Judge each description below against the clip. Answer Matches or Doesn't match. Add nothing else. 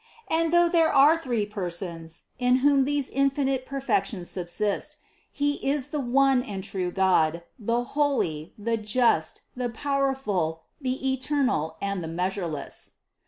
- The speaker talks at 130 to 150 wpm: Matches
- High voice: Matches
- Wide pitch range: Matches